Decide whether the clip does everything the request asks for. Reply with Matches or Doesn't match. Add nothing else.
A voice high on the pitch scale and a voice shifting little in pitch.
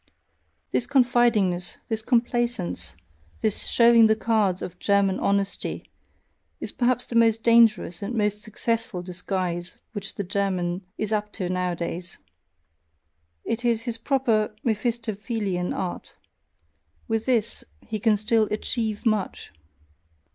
Doesn't match